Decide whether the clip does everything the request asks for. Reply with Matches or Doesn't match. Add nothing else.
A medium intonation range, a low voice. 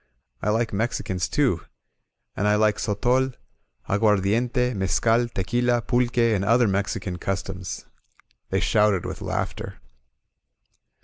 Matches